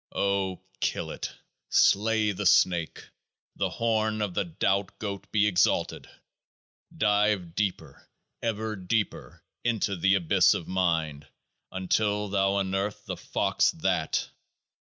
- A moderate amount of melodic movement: No, narrow, 2.3 semitones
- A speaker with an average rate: No, slow, 115 wpm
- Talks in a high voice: No, low, 100 Hz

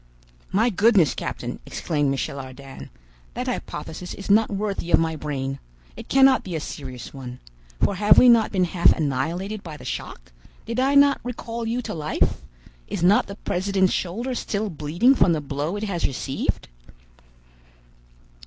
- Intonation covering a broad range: Yes, wide, 6.6 semitones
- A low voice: No, medium, 180 Hz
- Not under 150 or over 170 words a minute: Yes, average, 160 wpm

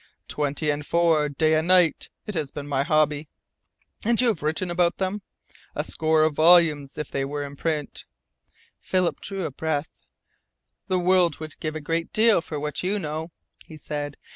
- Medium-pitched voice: Yes, medium, 155 Hz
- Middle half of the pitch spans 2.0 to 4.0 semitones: Yes, average, 3.0 semitones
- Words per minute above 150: Yes, average, 185 wpm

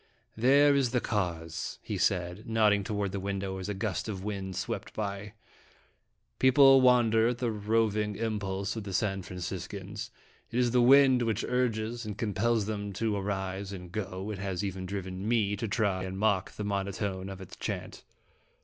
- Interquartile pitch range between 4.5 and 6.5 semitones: No, average, 2.8 semitones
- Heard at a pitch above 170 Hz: No, low, 105 Hz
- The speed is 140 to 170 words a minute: No, average, 180 wpm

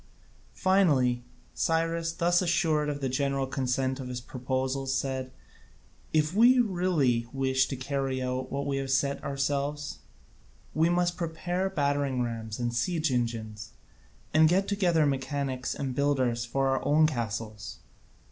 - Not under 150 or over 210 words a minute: No, average, 140 wpm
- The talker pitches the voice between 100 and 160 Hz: Yes, medium, 140 Hz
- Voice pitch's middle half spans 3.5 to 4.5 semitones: Yes, average, 3.8 semitones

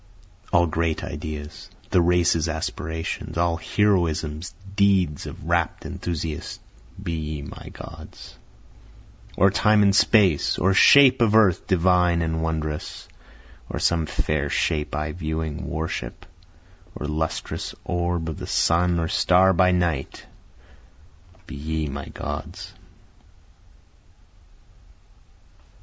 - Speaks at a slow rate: Yes, slow, 110 wpm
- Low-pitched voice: Yes, very low, 80 Hz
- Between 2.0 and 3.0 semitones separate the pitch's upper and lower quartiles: Yes, narrow, 2.6 semitones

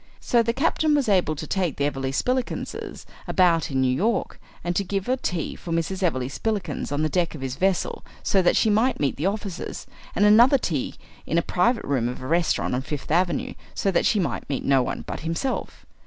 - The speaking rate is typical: No, fast, 215 wpm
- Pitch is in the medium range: Yes, medium, 175 Hz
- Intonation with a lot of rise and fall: Yes, wide, 6.2 semitones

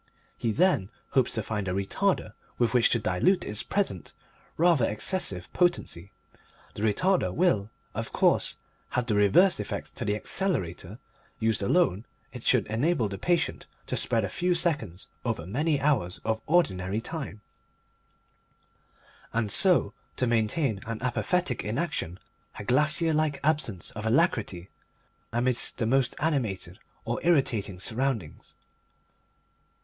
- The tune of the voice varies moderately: No, wide, 7.6 semitones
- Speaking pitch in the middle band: No, low, 115 Hz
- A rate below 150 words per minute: Yes, slow, 135 wpm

